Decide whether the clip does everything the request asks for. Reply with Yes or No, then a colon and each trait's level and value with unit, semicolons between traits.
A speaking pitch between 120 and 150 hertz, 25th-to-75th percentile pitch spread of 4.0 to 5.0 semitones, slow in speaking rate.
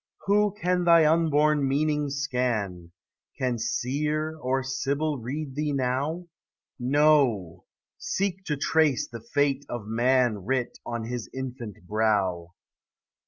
Yes: low, 135 Hz; average, 4.3 semitones; slow, 120 wpm